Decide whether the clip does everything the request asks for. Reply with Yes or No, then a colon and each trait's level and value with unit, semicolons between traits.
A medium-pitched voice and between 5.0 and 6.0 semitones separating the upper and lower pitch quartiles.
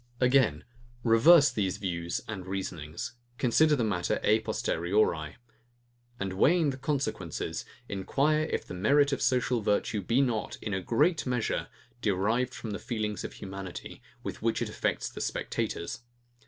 No: low, 110 Hz; wide, 5.5 semitones